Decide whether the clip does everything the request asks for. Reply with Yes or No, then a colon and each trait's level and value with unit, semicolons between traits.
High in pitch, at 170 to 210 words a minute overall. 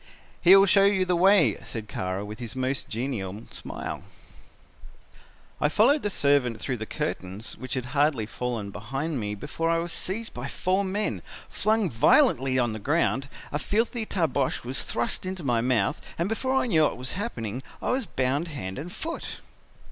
No: medium, 140 Hz; average, 180 wpm